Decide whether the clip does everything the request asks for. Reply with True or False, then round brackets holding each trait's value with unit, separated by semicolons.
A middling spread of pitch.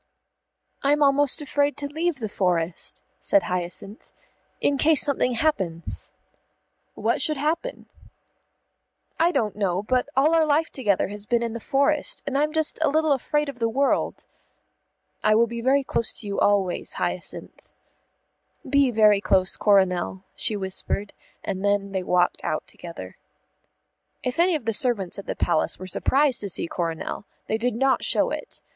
False (6.3 semitones)